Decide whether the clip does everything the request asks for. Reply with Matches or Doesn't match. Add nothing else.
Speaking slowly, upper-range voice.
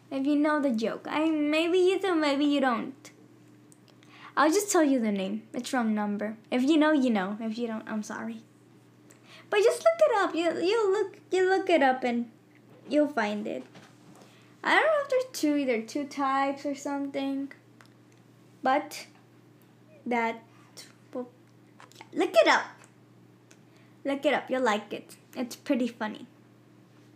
Doesn't match